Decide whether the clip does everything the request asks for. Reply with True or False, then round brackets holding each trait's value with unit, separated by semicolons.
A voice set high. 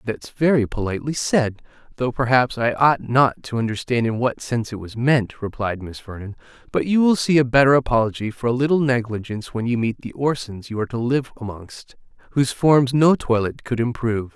False (120 Hz)